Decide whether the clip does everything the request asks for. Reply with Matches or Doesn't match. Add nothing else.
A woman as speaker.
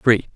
Doesn't match